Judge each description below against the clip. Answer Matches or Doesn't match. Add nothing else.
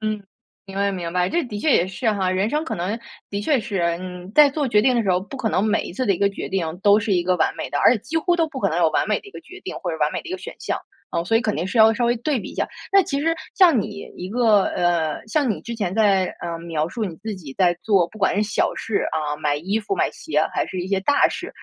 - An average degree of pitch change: Matches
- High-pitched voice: Matches